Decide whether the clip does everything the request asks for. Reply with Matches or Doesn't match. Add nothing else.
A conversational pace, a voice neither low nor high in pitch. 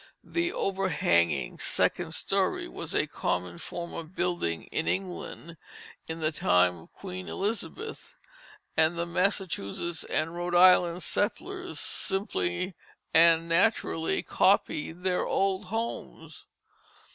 Doesn't match